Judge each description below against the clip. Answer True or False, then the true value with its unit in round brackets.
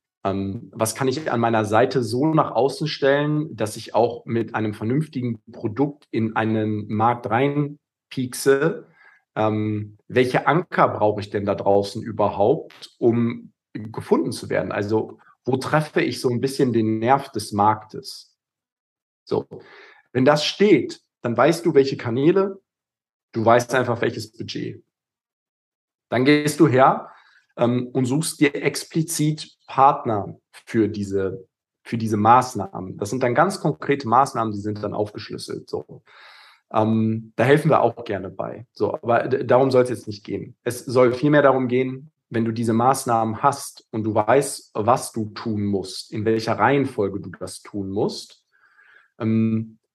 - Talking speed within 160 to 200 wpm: False (150 wpm)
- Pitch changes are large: False (4.0 semitones)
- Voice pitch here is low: True (120 Hz)